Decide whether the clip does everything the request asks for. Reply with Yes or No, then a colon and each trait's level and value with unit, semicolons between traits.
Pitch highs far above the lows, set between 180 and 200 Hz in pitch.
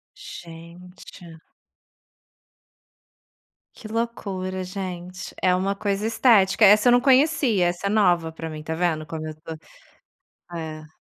No: average, 4.1 semitones; medium, 185 Hz